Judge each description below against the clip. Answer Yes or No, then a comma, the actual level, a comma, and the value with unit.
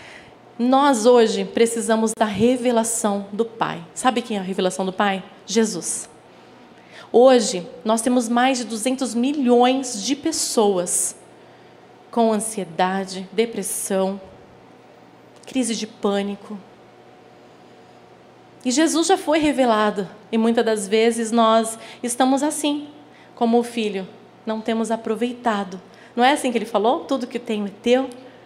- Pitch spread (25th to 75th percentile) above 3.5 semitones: No, average, 3.2 semitones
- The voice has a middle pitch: No, high, 230 Hz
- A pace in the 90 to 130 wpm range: Yes, average, 125 wpm